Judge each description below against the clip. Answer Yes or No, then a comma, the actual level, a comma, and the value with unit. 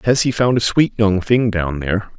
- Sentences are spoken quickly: Yes, fast, 245 wpm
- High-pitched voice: No, low, 105 Hz